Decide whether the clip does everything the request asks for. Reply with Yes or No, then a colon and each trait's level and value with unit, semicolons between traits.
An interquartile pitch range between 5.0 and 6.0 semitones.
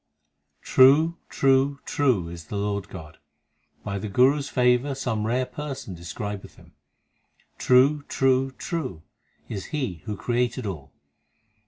Yes: average, 5.3 semitones